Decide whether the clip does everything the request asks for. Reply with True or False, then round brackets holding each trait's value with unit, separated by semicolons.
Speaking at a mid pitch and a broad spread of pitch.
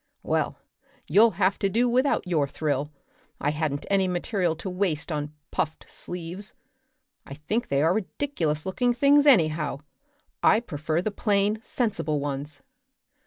True (175 Hz; 5.9 semitones)